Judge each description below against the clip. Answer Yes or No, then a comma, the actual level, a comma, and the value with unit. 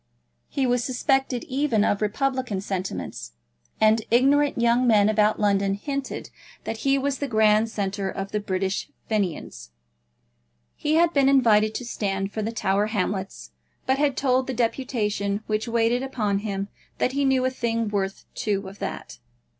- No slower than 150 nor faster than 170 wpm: Yes, average, 160 wpm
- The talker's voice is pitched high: Yes, high, 220 Hz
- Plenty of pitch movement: No, average, 4.4 semitones